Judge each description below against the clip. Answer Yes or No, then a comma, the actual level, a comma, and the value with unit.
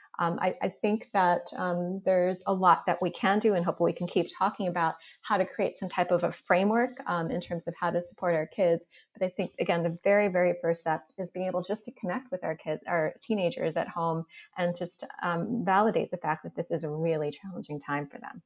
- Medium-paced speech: No, fast, 240 wpm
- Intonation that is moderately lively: No, narrow, 2.3 semitones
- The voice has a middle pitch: Yes, medium, 180 Hz